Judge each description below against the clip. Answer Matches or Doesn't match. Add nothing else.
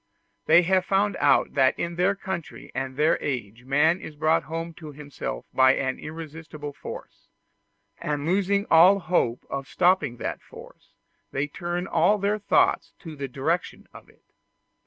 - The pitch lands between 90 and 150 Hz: Doesn't match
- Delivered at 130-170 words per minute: Matches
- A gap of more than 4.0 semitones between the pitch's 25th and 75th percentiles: Matches